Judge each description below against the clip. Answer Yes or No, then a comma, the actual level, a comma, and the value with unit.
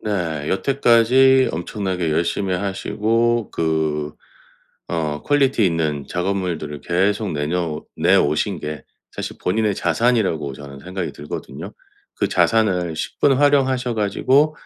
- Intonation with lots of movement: Yes, wide, 6.5 semitones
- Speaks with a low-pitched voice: Yes, very low, 95 Hz